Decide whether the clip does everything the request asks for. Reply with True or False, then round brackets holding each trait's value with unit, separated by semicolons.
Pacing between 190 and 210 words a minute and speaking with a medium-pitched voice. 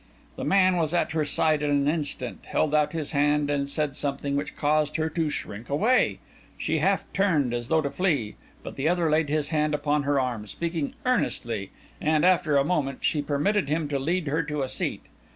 True (205 wpm; 150 Hz)